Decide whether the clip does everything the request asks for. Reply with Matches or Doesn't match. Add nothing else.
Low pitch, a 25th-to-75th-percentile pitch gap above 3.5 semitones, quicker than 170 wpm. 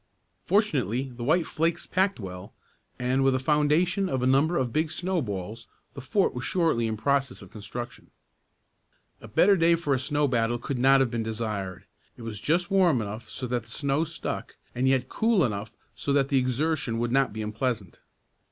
Matches